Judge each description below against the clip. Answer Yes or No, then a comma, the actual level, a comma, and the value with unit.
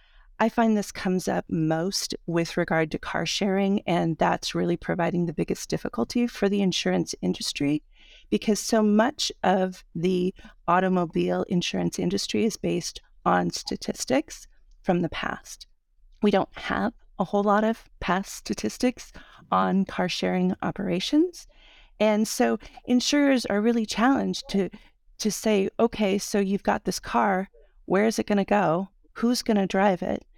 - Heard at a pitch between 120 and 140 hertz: No, high, 195 Hz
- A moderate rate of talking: Yes, average, 150 wpm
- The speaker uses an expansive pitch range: No, average, 3.7 semitones